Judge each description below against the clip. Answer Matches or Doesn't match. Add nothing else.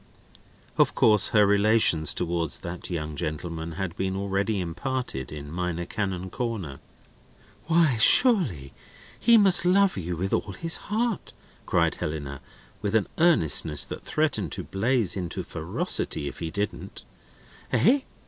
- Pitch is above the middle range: Doesn't match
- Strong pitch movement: Matches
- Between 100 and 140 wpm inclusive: Matches